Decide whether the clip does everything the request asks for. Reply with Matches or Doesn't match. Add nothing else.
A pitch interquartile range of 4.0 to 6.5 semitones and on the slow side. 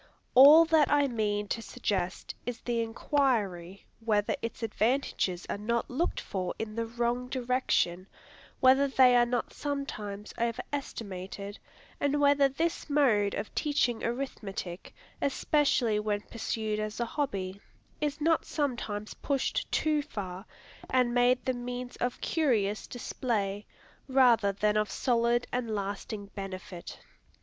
Matches